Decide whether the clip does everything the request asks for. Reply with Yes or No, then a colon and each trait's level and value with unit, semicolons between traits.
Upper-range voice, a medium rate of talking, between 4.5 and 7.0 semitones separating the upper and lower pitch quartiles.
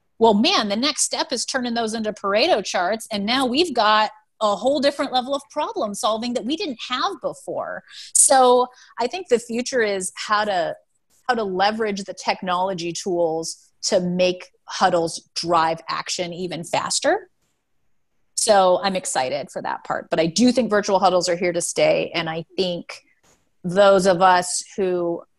Yes: high, 205 Hz; average, 170 wpm; wide, 5.6 semitones